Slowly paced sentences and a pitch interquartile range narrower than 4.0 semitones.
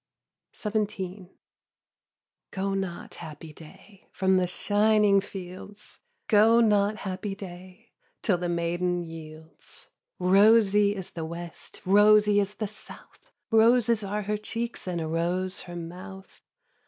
Yes: slow, 120 wpm; average, 3.0 semitones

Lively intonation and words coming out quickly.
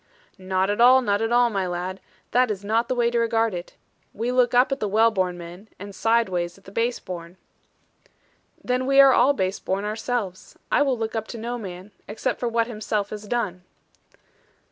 No: average, 4.0 semitones; fast, 210 wpm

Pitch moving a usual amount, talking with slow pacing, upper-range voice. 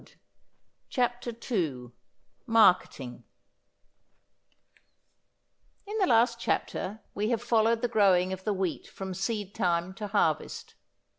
Yes: average, 4.0 semitones; slow, 105 wpm; high, 205 Hz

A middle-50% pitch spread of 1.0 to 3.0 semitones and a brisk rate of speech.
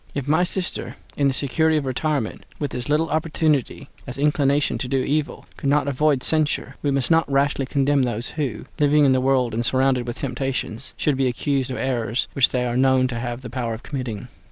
Yes: narrow, 2.6 semitones; fast, 210 wpm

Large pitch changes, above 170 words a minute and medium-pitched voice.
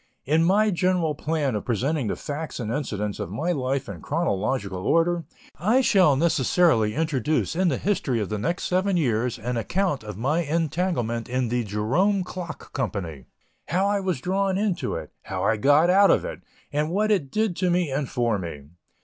Yes: wide, 7.3 semitones; average, 185 wpm; medium, 150 Hz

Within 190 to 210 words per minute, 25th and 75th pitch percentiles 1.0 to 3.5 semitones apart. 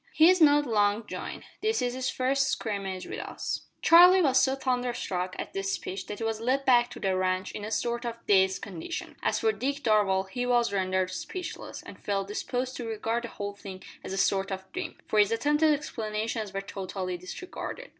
No: average, 200 wpm; average, 5.2 semitones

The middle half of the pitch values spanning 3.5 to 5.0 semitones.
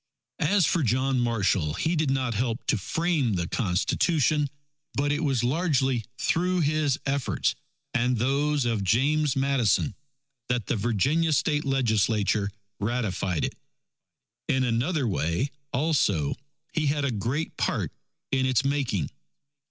Yes: average, 4.7 semitones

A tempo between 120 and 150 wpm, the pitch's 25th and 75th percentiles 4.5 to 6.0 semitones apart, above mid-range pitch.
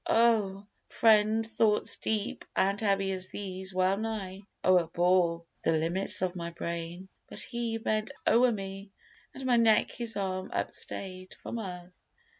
No: average, 140 wpm; average, 3.1 semitones; high, 195 Hz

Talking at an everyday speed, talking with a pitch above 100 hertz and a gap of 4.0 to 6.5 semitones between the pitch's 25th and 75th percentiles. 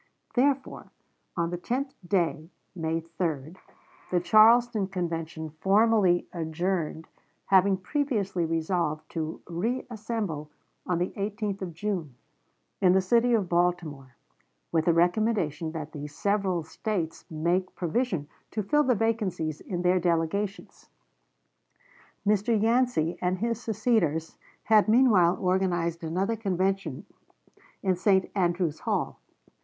No: slow, 115 wpm; medium, 185 Hz; average, 4.4 semitones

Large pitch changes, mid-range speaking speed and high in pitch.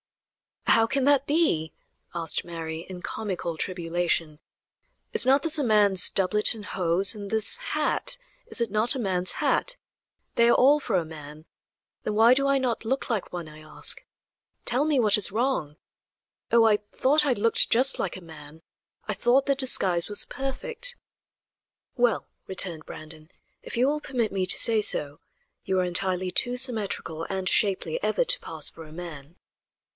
Yes: wide, 6.8 semitones; average, 170 wpm; high, 210 Hz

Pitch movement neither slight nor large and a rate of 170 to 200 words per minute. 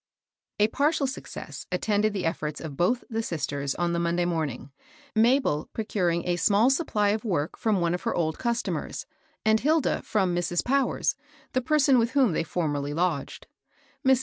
No: wide, 6.4 semitones; average, 175 wpm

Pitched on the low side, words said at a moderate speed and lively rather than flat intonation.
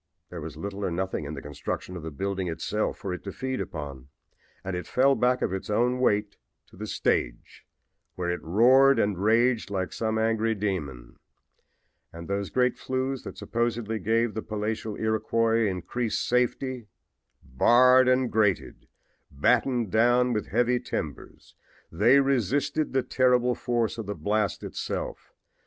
No: low, 110 Hz; average, 155 wpm; average, 4.6 semitones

